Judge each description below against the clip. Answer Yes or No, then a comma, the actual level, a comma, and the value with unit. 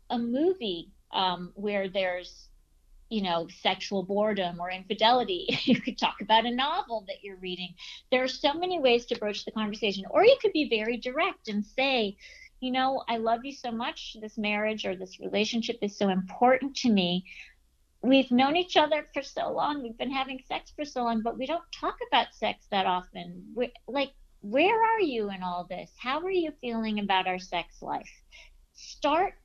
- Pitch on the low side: No, high, 230 Hz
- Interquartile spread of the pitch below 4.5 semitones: No, average, 5.3 semitones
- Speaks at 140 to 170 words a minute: No, average, 190 wpm